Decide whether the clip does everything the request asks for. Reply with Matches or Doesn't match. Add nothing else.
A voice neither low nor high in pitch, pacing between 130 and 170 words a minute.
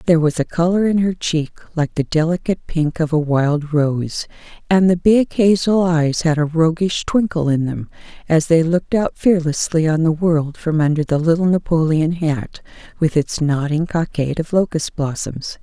Doesn't match